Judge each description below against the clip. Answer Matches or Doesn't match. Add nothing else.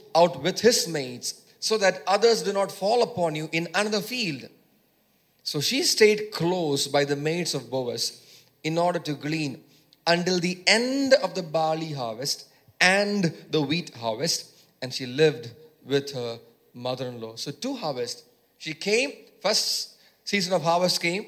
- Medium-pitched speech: Matches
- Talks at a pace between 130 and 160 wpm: Matches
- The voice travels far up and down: Matches